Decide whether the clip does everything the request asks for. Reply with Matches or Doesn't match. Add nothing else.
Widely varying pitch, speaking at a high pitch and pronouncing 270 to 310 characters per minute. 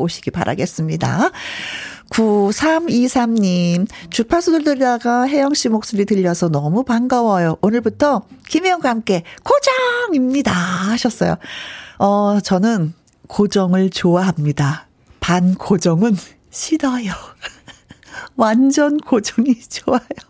Doesn't match